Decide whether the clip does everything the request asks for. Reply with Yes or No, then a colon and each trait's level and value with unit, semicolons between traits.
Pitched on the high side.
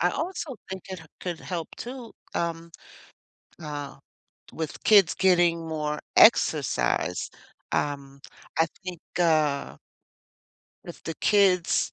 No: medium, 170 Hz